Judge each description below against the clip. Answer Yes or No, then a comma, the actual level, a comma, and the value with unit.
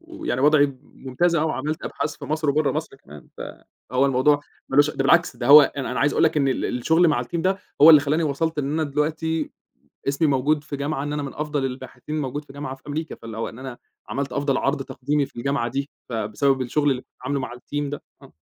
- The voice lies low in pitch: No, medium, 145 Hz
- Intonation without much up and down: Yes, narrow, 2.3 semitones